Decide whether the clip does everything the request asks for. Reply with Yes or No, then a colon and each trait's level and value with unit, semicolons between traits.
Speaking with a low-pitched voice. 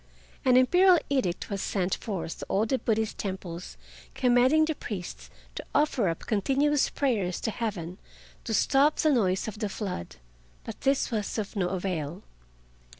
No: high, 215 Hz